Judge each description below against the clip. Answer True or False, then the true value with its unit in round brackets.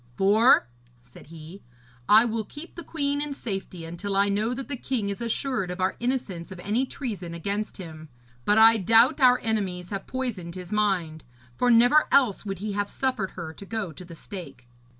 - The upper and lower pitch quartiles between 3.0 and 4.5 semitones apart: False (5.1 semitones)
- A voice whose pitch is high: True (205 Hz)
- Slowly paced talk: False (190 wpm)